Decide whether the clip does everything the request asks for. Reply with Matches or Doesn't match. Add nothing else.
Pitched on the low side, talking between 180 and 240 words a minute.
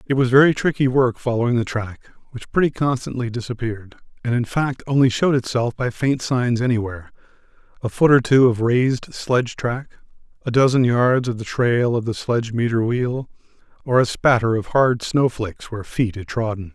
Matches